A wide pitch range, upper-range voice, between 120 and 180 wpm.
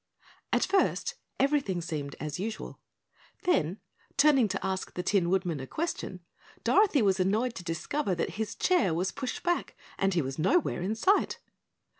Yes: wide, 7.9 semitones; high, 195 Hz; average, 160 wpm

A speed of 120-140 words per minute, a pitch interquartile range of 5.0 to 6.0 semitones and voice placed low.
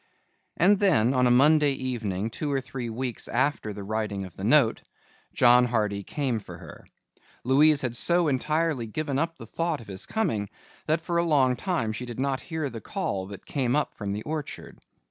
No: average, 195 wpm; wide, 5.5 semitones; low, 130 Hz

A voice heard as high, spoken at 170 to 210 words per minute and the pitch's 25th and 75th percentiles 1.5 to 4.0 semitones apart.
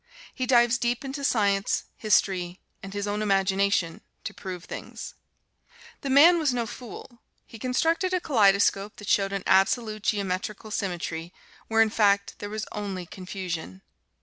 No: high, 205 Hz; average, 150 wpm; average, 3.7 semitones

